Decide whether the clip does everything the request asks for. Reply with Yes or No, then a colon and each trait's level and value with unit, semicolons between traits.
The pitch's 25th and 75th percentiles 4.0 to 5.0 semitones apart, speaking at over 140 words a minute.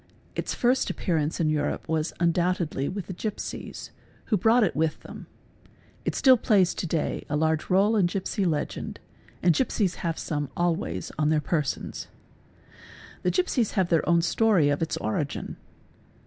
Yes: average, 4.3 semitones; average, 170 wpm